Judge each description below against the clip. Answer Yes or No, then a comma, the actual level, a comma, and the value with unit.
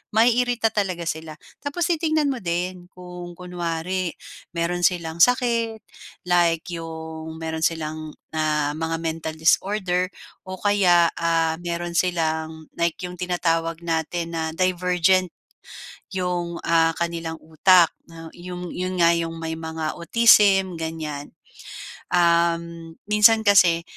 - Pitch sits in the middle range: Yes, medium, 170 Hz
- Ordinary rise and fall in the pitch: No, narrow, 2.0 semitones